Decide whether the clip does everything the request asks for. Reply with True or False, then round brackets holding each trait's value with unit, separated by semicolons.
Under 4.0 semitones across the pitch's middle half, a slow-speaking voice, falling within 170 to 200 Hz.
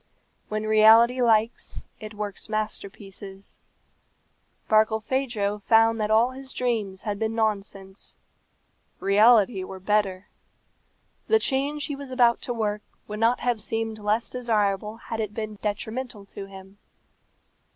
False (2.4 semitones; 125 wpm; 215 Hz)